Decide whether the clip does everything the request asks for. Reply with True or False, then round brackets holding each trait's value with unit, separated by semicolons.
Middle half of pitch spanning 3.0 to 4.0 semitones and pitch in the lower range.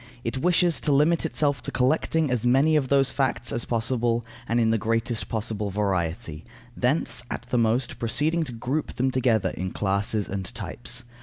True (3.7 semitones; 120 Hz)